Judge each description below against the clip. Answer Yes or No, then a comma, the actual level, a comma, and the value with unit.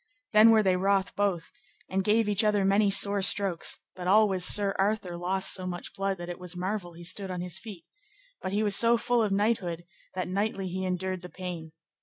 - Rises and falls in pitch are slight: Yes, narrow, 2.2 semitones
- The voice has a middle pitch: No, high, 195 Hz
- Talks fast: Yes, fast, 210 wpm